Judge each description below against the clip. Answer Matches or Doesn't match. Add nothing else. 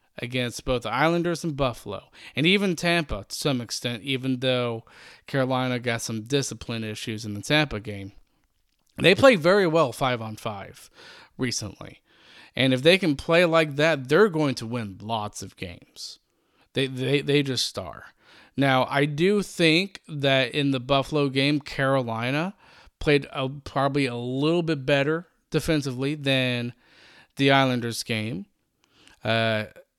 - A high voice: Doesn't match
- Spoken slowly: Doesn't match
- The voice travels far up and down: Doesn't match